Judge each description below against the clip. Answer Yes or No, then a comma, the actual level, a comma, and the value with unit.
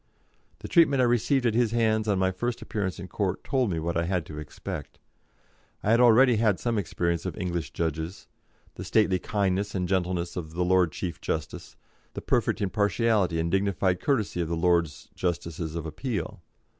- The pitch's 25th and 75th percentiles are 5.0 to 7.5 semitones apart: No, average, 4.3 semitones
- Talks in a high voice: No, very low, 95 Hz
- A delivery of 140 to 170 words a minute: No, average, 180 wpm